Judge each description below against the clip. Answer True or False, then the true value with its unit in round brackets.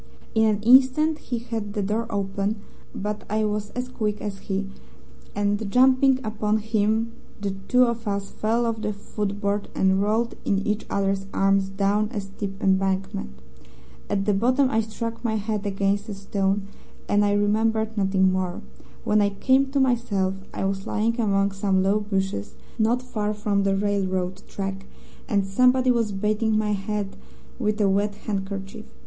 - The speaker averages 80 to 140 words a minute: False (165 wpm)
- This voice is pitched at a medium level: False (205 Hz)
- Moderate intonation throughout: False (2.1 semitones)